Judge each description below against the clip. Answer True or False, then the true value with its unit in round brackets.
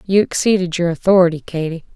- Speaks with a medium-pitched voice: True (175 Hz)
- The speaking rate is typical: True (155 wpm)